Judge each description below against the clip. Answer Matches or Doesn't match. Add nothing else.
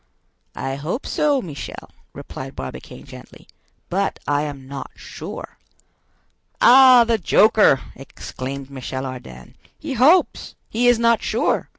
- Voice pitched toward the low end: Doesn't match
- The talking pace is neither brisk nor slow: Doesn't match